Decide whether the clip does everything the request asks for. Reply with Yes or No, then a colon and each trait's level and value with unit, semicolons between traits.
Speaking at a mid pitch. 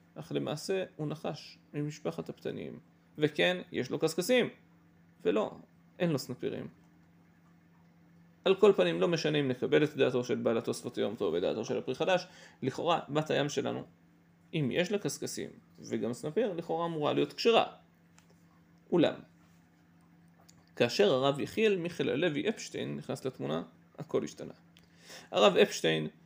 Yes: medium, 165 Hz